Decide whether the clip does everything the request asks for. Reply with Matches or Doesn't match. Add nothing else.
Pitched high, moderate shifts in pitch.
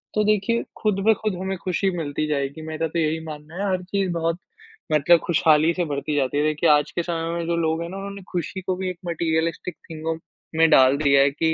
Doesn't match